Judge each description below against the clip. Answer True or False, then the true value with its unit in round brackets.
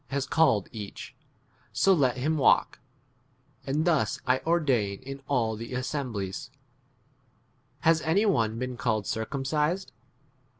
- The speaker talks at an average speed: False (130 wpm)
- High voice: False (135 Hz)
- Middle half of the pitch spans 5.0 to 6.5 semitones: True (5.3 semitones)